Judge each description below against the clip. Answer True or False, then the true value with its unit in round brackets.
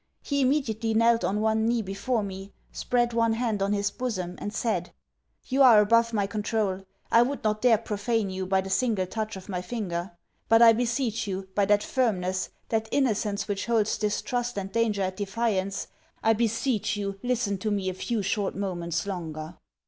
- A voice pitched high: True (210 Hz)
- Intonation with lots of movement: False (3.0 semitones)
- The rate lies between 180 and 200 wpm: True (185 wpm)